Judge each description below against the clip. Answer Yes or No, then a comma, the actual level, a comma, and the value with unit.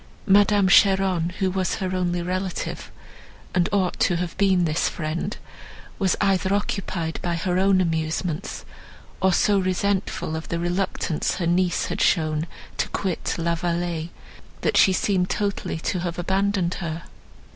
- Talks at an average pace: Yes, average, 145 wpm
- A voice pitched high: No, medium, 180 Hz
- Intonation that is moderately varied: No, narrow, 2.2 semitones